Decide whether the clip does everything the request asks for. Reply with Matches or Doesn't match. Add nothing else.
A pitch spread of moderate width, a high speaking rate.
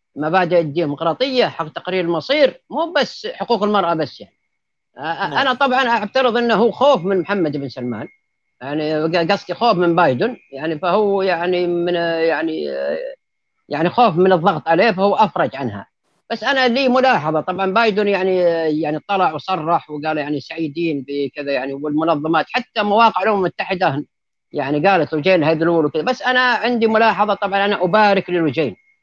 Doesn't match